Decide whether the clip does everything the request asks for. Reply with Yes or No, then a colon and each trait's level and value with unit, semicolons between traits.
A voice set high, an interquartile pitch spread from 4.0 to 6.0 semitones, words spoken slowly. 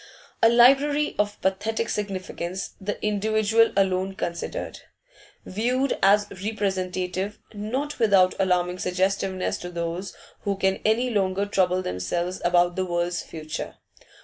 No: high, 195 Hz; average, 3.0 semitones; slow, 120 wpm